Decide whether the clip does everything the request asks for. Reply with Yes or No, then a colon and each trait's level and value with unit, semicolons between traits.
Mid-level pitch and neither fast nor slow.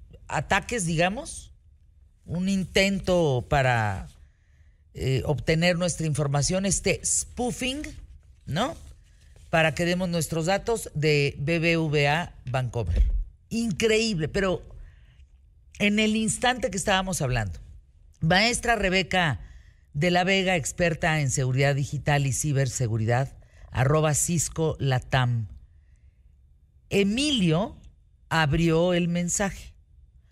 No: medium, 150 Hz; slow, 90 wpm